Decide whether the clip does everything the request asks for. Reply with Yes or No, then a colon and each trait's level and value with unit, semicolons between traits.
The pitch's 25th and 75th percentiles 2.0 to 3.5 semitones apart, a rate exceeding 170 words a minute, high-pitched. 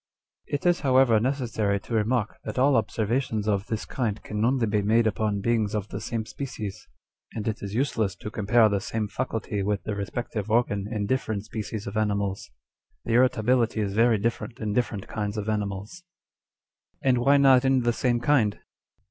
No: average, 2.8 semitones; average, 190 wpm; low, 110 Hz